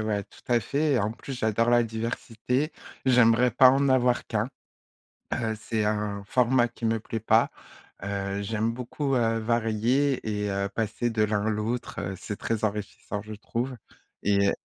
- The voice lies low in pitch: Yes, low, 115 Hz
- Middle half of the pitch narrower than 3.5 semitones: Yes, narrow, 2.6 semitones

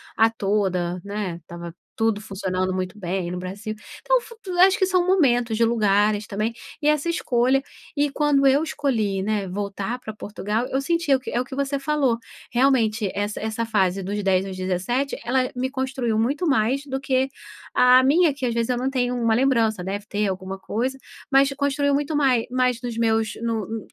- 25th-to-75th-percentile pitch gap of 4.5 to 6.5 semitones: Yes, average, 4.8 semitones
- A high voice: Yes, high, 230 Hz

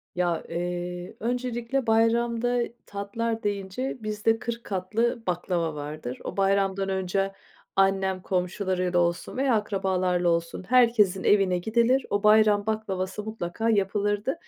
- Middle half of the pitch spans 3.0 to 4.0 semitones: Yes, average, 3.7 semitones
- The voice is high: Yes, high, 200 Hz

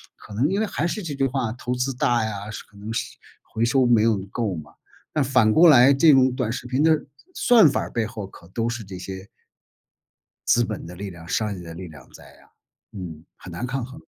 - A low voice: Yes, low, 115 Hz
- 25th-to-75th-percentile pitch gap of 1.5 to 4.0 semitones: No, average, 5.0 semitones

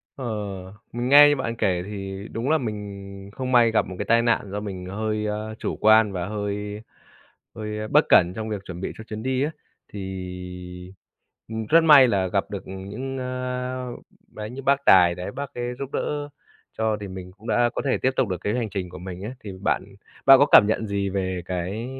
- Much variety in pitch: No, average, 4.3 semitones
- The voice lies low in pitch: Yes, low, 105 Hz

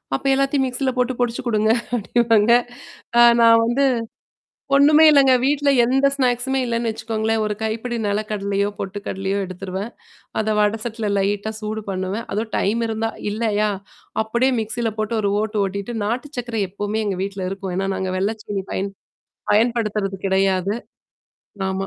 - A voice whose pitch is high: Yes, high, 220 Hz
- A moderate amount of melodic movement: Yes, average, 3.0 semitones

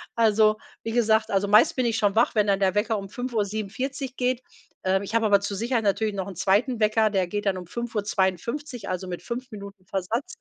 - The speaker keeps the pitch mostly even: No, average, 3.0 semitones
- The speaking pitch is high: Yes, high, 215 Hz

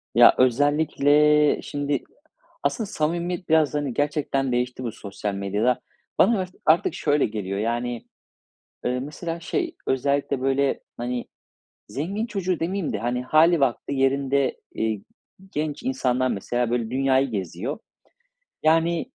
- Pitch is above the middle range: No, medium, 140 Hz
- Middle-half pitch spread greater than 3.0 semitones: Yes, average, 4.2 semitones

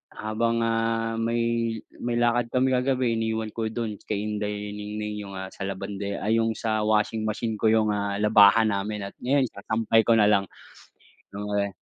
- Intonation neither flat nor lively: No, narrow, 1.7 semitones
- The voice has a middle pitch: No, low, 110 Hz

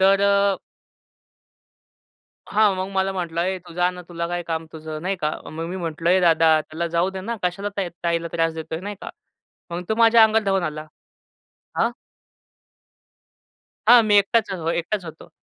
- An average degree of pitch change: Yes, average, 3.1 semitones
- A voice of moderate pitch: Yes, medium, 180 Hz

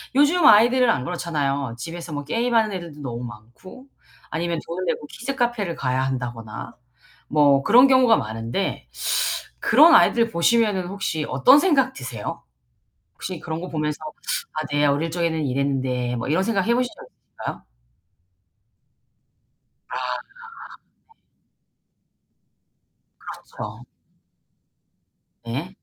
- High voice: No, medium, 165 Hz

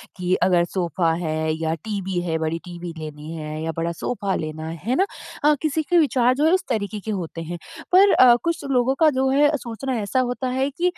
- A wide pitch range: Yes, wide, 8.4 semitones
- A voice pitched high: Yes, high, 205 Hz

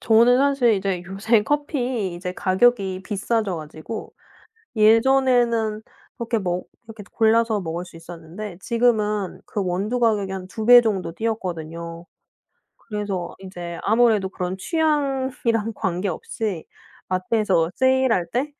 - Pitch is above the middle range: Yes, high, 210 Hz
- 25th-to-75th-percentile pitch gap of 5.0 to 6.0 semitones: No, average, 4.3 semitones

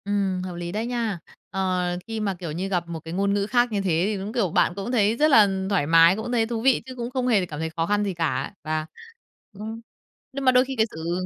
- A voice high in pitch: Yes, high, 200 Hz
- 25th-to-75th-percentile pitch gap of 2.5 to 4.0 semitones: No, average, 4.8 semitones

